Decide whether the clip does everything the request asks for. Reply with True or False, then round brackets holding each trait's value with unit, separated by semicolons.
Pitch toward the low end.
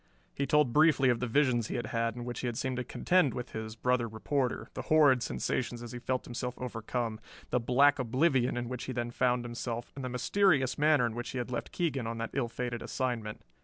True (125 Hz)